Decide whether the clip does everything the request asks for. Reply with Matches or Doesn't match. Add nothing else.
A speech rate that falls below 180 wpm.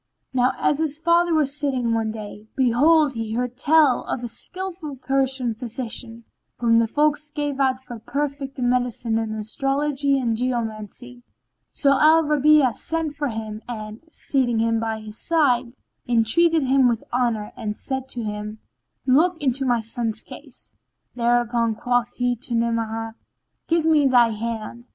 Matches